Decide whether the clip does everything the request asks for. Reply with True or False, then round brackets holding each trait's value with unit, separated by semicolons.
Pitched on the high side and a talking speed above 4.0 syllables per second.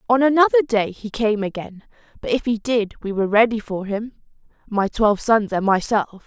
True (220 Hz; 5.4 syllables/s)